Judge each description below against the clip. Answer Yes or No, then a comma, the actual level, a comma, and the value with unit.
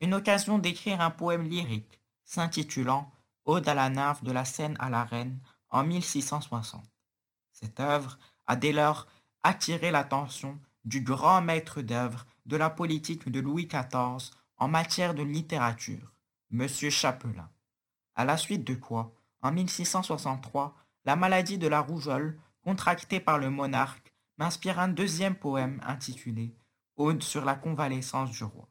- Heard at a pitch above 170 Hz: No, medium, 140 Hz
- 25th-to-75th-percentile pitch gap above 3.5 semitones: Yes, average, 4.5 semitones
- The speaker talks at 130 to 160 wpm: Yes, slow, 145 wpm